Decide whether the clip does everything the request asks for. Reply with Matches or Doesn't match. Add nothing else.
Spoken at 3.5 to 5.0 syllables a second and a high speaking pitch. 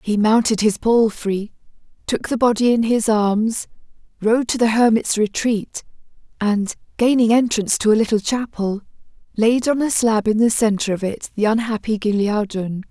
Matches